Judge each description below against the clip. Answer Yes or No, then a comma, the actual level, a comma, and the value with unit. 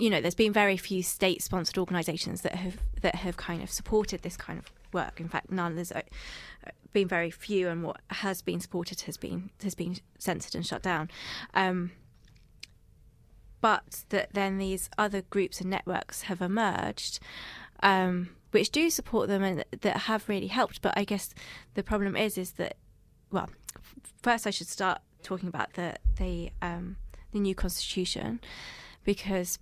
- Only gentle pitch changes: Yes, narrow, 2.2 semitones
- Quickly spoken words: No, average, 165 wpm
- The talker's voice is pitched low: No, medium, 185 Hz